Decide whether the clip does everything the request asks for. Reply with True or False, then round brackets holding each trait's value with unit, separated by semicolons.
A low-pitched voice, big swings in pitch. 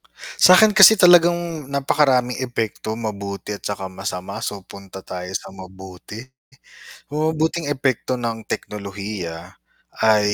True (110 Hz; 7.6 semitones)